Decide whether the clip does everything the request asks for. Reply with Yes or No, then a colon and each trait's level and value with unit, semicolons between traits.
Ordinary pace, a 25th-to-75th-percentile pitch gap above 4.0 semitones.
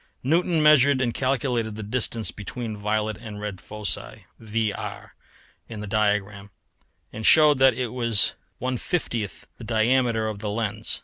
No: average, 145 wpm; average, 3.3 semitones